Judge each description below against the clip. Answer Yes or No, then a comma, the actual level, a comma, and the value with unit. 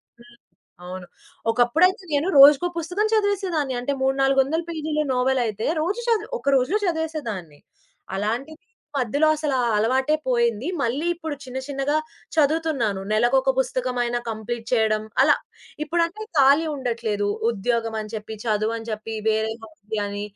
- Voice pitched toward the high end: Yes, very high, 260 Hz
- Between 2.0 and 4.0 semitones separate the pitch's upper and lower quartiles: No, wide, 5.7 semitones